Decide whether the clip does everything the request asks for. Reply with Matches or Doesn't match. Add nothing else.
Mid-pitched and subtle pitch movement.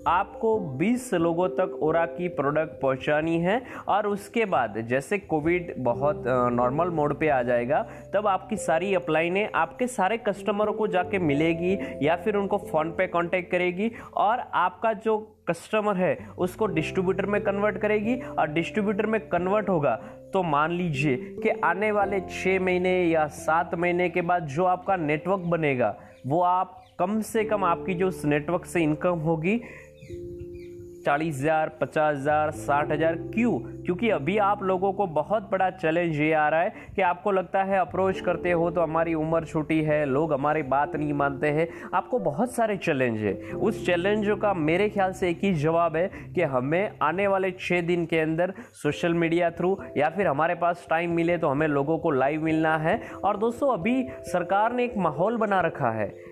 Doesn't match